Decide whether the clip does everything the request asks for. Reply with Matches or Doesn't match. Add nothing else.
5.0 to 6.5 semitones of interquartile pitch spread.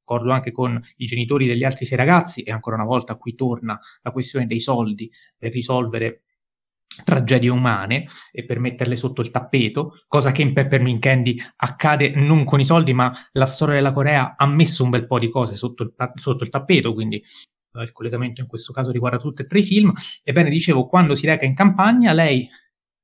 Doesn't match